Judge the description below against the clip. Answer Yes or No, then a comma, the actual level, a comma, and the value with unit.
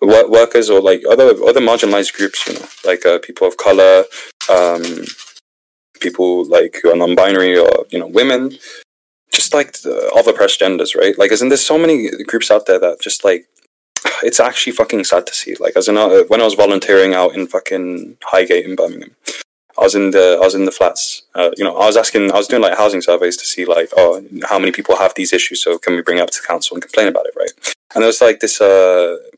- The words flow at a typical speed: No, fast, 230 wpm